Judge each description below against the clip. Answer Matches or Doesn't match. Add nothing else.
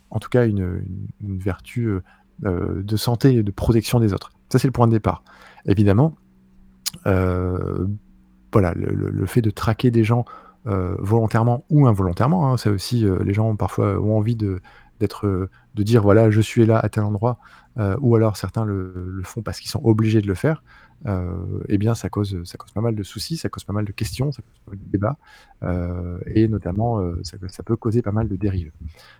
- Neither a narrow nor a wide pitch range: Matches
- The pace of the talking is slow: Doesn't match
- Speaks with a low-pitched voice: Matches